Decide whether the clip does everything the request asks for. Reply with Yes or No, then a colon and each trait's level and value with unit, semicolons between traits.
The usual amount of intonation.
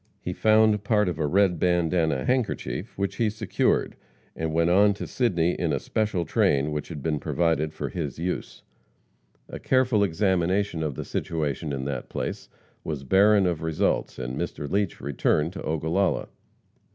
Yes: average, 4.7 semitones